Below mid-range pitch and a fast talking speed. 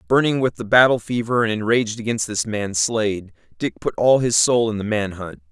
Yes: low, 110 Hz; fast, 215 wpm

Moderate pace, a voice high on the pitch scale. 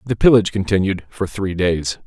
No: average, 175 wpm; very low, 95 Hz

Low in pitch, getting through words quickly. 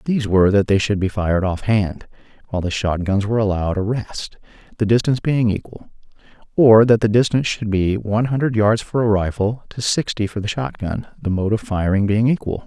Yes: low, 105 Hz; fast, 215 wpm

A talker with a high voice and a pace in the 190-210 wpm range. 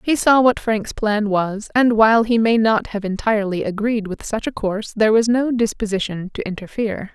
Yes: high, 215 Hz; average, 200 wpm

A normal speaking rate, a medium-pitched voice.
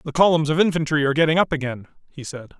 No: fast, 230 wpm; medium, 150 Hz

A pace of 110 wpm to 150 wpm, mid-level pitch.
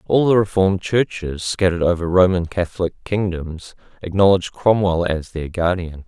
No: average, 140 wpm; very low, 90 Hz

